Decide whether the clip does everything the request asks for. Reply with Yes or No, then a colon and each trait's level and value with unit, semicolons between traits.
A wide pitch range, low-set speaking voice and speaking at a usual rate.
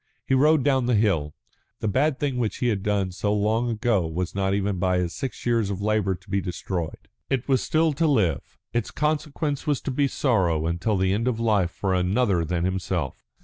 No: wide, 5.7 semitones; low, 105 Hz; fast, 210 wpm